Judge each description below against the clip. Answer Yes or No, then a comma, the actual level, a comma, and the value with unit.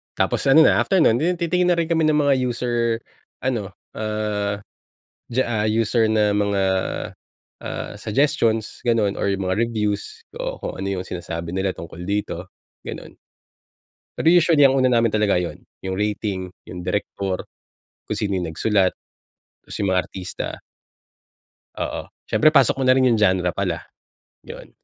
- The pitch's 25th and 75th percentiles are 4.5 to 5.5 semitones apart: Yes, average, 4.8 semitones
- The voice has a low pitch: Yes, low, 105 Hz